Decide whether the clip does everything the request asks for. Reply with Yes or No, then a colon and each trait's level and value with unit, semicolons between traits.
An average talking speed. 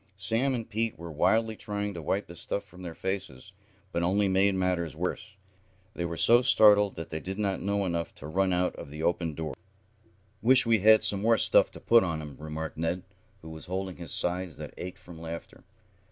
No: fast, 210 wpm